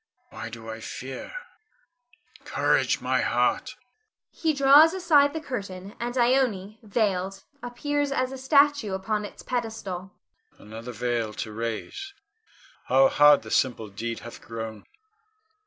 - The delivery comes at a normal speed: No, slow, 125 wpm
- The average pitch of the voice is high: Yes, high, 205 Hz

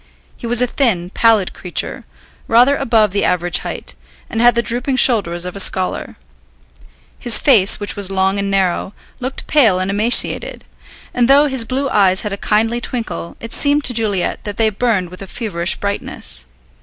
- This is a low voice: No, high, 215 Hz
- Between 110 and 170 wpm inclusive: No, average, 180 wpm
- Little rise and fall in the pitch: No, average, 4.2 semitones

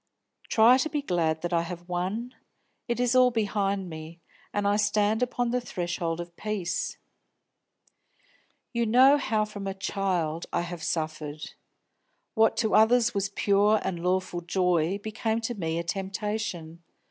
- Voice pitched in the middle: No, high, 195 Hz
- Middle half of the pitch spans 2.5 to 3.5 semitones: No, average, 4.3 semitones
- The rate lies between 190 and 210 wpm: No, average, 150 wpm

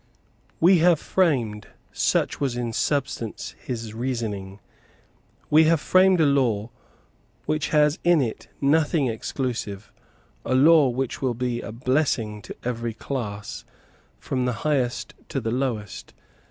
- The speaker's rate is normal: No, slow, 130 wpm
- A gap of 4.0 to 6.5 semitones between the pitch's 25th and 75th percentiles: Yes, average, 4.6 semitones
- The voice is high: No, low, 125 Hz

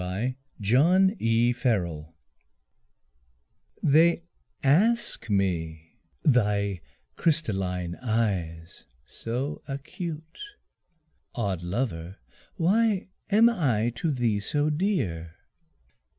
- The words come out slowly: Yes, slow, 70 wpm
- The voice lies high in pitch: No, low, 120 Hz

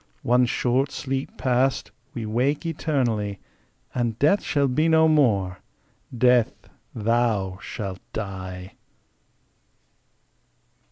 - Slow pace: Yes, slow, 95 wpm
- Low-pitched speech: Yes, low, 120 Hz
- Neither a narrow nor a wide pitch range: Yes, average, 4.6 semitones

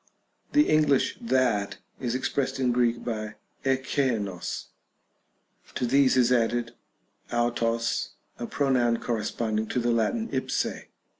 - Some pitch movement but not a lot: No, narrow, 2.2 semitones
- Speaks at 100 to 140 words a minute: Yes, slow, 135 wpm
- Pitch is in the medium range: No, low, 120 Hz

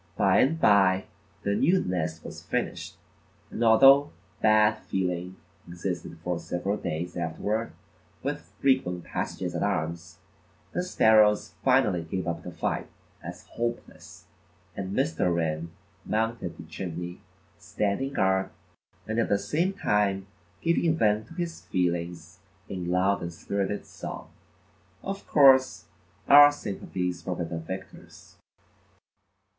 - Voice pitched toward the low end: Yes, very low, 95 Hz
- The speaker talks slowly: Yes, slow, 125 wpm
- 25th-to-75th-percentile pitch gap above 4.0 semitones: Yes, average, 4.8 semitones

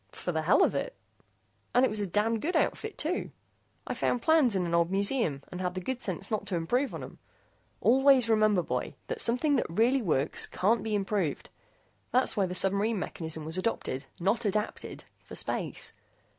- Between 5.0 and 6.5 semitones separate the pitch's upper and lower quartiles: Yes, wide, 5.5 semitones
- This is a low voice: No, high, 210 Hz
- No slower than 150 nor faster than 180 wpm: No, average, 190 wpm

